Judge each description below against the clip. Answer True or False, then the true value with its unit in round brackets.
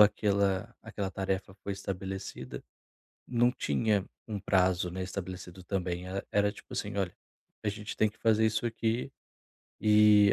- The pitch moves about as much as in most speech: False (2.2 semitones)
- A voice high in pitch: False (100 Hz)